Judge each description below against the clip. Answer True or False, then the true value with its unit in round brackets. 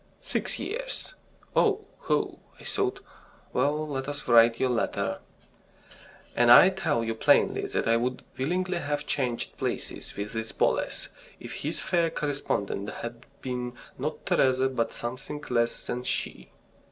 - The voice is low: True (130 Hz)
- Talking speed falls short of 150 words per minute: True (140 wpm)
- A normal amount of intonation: True (4.4 semitones)